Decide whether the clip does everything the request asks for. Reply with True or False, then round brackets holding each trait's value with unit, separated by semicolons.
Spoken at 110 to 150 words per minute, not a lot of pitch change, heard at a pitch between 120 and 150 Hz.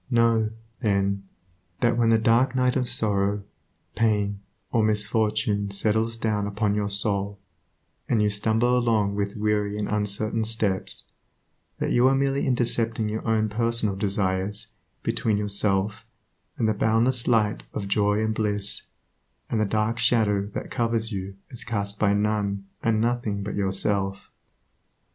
False (145 wpm; 2.1 semitones; 105 Hz)